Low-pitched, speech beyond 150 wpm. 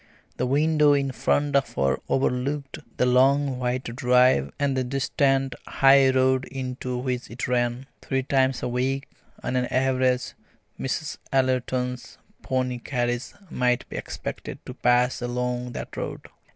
No: low, 130 Hz; average, 140 wpm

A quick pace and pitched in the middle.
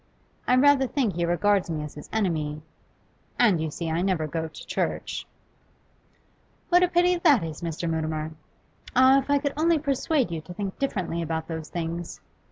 No: average, 175 wpm; medium, 175 Hz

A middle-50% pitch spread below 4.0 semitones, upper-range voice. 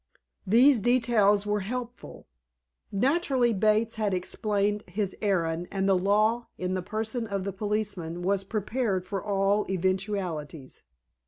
Yes: average, 2.7 semitones; high, 205 Hz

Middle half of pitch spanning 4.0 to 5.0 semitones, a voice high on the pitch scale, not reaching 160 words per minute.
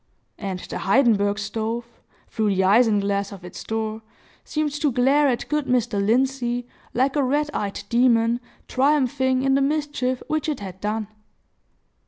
Yes: average, 4.4 semitones; high, 240 Hz; average, 150 wpm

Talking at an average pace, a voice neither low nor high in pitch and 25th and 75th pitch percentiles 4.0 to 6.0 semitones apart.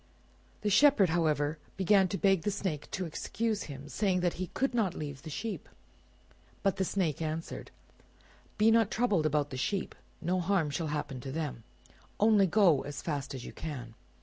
Yes: average, 175 wpm; medium, 175 Hz; average, 5.2 semitones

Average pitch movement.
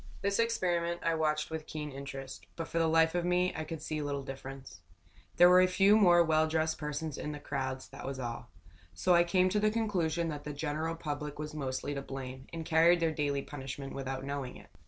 Yes: average, 3.6 semitones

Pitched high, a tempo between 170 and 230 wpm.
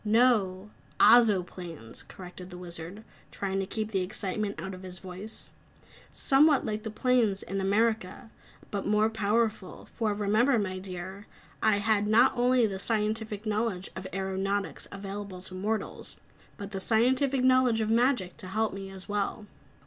No: high, 205 Hz; average, 150 wpm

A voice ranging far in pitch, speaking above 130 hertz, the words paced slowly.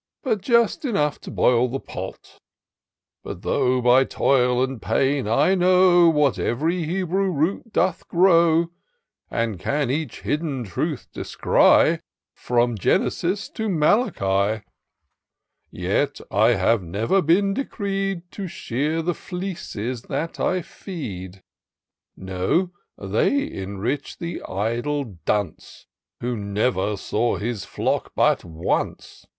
Yes: wide, 8.3 semitones; medium, 140 Hz; slow, 115 wpm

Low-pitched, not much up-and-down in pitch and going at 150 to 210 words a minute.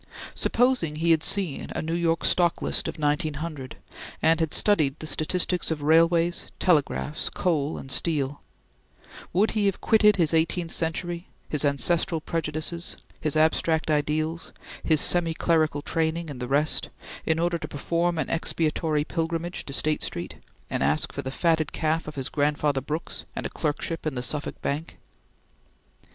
No: medium, 160 Hz; narrow, 2.2 semitones; average, 160 wpm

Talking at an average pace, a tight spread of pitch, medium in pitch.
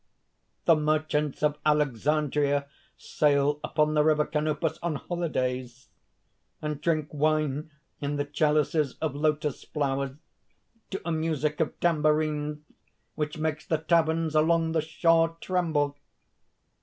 No: slow, 120 wpm; narrow, 1.4 semitones; medium, 150 Hz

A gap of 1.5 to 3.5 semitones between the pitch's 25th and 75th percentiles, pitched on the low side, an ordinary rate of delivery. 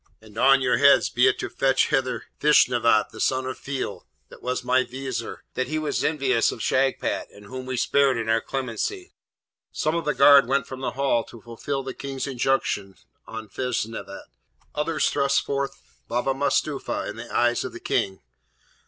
Yes: average, 2.9 semitones; low, 130 Hz; average, 180 wpm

